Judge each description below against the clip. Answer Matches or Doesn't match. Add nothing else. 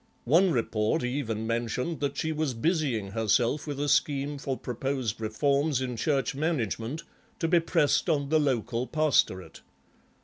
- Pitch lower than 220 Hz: Matches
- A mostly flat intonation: Doesn't match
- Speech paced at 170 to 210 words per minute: Doesn't match